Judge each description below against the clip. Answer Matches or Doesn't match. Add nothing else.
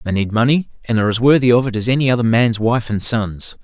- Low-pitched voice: Matches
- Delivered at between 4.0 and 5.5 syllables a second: Doesn't match